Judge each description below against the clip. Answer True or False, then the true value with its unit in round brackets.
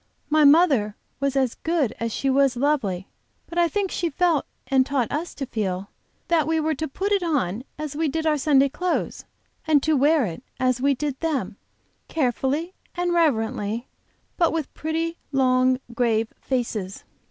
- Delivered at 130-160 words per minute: False (170 wpm)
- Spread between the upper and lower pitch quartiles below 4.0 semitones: False (4.4 semitones)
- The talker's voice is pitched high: True (280 Hz)